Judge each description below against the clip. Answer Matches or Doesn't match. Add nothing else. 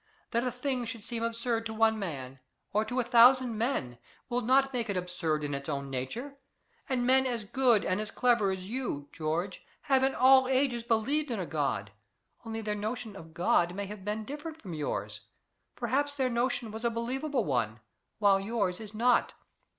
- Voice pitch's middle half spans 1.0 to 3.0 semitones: Doesn't match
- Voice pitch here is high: Matches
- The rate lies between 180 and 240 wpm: Matches